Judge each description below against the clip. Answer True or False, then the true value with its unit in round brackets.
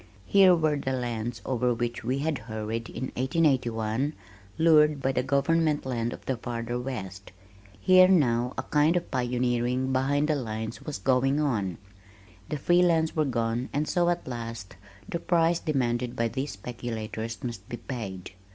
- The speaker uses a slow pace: False (160 wpm)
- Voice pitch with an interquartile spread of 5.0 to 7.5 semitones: False (4.4 semitones)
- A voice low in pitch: True (125 Hz)